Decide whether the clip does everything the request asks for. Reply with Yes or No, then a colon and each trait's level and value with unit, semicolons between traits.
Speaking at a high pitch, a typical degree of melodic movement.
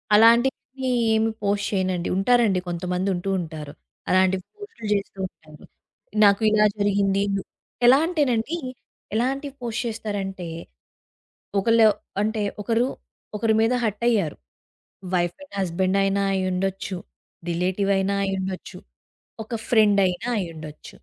Yes: high, 200 Hz; average, 3.4 semitones